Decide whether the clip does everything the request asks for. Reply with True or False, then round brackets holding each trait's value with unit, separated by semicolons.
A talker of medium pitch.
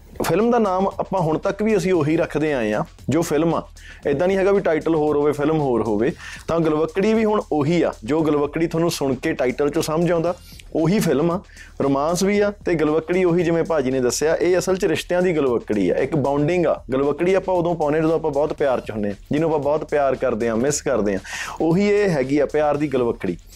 True (155 Hz)